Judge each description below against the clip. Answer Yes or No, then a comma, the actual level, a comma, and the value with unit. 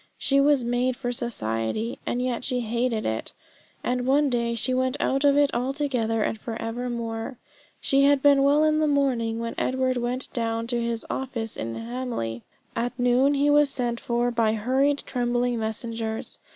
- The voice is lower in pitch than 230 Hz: No, high, 245 Hz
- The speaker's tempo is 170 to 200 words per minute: Yes, average, 175 wpm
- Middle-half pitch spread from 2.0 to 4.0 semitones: Yes, average, 2.8 semitones